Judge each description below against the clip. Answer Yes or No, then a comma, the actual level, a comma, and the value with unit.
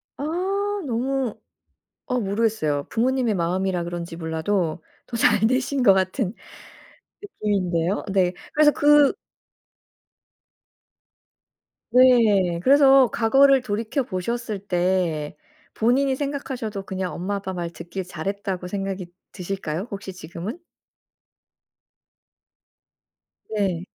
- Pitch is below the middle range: No, high, 200 Hz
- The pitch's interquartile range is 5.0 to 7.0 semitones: Yes, wide, 5.4 semitones